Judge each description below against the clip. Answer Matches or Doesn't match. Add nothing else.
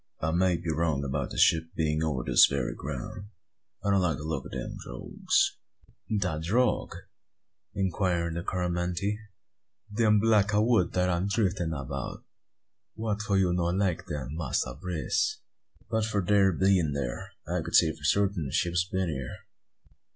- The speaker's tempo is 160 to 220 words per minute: Matches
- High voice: Doesn't match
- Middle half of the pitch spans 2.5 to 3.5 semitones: Doesn't match